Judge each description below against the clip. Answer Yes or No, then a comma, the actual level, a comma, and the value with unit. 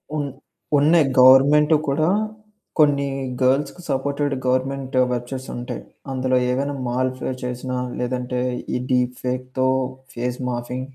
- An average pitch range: No, narrow, 2.0 semitones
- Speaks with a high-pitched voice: No, low, 130 Hz